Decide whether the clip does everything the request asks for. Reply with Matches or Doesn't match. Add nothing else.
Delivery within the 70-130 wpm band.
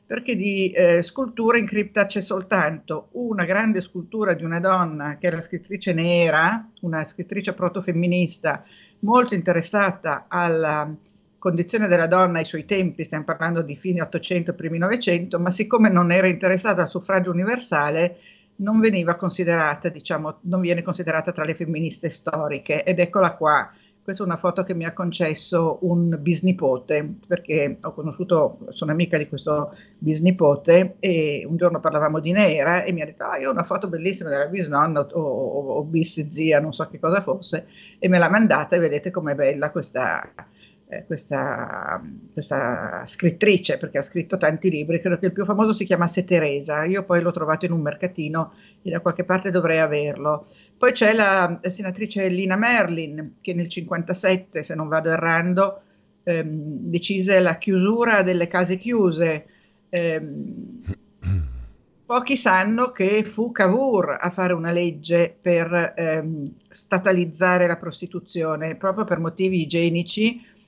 Doesn't match